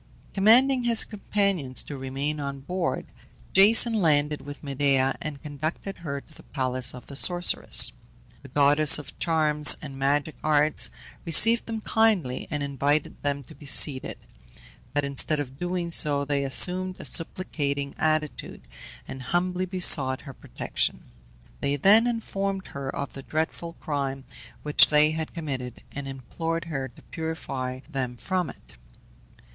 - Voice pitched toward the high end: No, medium, 150 Hz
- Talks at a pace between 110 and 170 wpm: Yes, average, 145 wpm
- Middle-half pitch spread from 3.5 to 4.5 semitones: Yes, average, 4.1 semitones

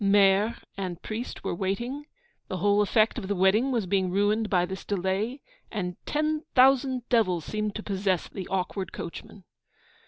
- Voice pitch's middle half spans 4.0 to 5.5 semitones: No, average, 3.3 semitones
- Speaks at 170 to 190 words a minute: No, average, 160 wpm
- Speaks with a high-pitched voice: Yes, high, 205 Hz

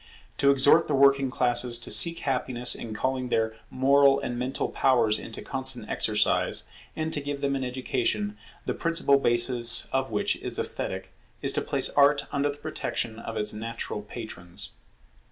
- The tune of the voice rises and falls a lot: No, average, 3.1 semitones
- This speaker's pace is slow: No, average, 165 wpm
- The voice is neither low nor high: No, low, 130 Hz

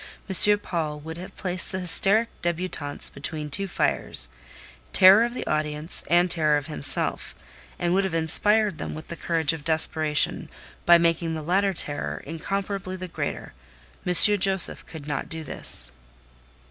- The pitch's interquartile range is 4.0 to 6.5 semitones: No, average, 3.6 semitones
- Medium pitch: Yes, medium, 165 Hz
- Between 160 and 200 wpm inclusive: No, average, 145 wpm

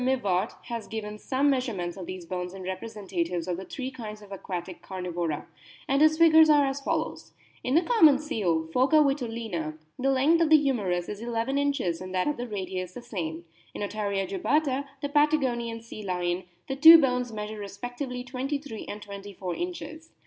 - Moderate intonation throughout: No, wide, 6.8 semitones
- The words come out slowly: No, average, 185 wpm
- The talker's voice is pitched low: No, high, 230 Hz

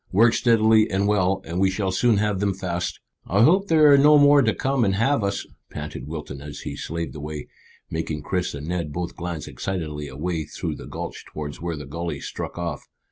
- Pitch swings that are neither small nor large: No, wide, 5.9 semitones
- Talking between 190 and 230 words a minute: Yes, fast, 205 wpm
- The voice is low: Yes, very low, 90 Hz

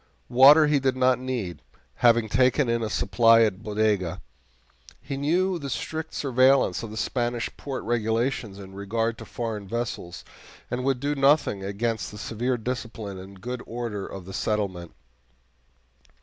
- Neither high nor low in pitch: No, low, 115 Hz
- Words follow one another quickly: No, average, 150 wpm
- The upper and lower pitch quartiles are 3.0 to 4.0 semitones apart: Yes, average, 3.7 semitones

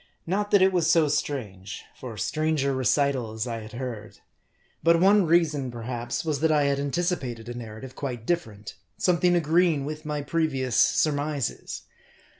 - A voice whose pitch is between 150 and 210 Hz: No, medium, 140 Hz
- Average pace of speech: Yes, average, 155 wpm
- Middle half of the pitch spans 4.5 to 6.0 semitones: Yes, average, 5.3 semitones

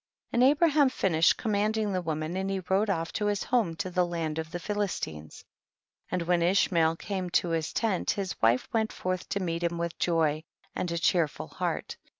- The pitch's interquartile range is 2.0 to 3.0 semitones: No, average, 3.6 semitones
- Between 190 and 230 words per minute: Yes, fast, 205 wpm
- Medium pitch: Yes, medium, 180 Hz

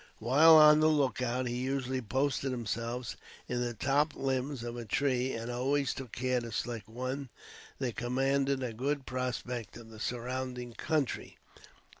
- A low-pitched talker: Yes, low, 125 Hz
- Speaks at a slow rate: No, average, 155 wpm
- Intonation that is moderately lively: No, narrow, 2.1 semitones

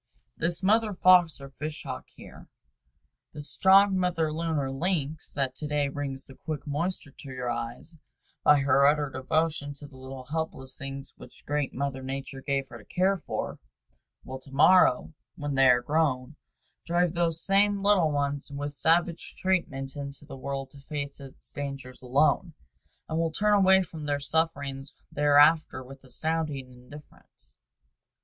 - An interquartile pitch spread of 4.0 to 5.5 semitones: No, average, 3.3 semitones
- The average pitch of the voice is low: No, medium, 145 Hz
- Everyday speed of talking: Yes, average, 160 wpm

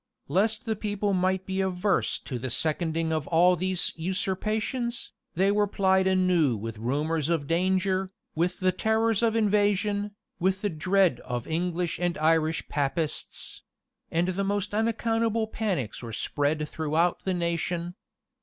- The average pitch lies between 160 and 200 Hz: Yes, medium, 185 Hz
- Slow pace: No, average, 145 wpm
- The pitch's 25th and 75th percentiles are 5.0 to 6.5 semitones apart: No, average, 4.0 semitones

